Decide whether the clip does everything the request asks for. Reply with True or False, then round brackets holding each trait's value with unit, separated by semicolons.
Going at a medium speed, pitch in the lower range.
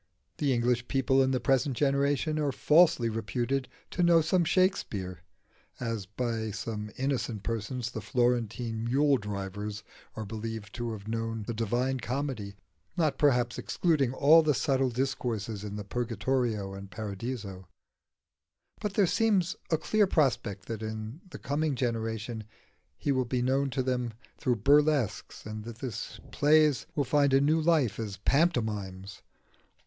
True (145 wpm; 125 Hz)